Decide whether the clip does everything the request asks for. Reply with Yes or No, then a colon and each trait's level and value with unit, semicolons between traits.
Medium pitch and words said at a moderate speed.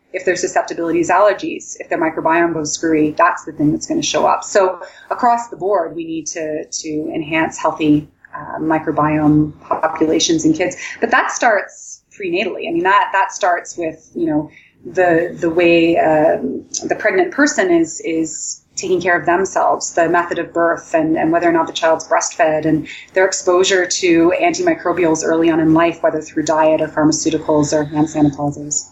Yes: medium, 170 Hz; average, 180 wpm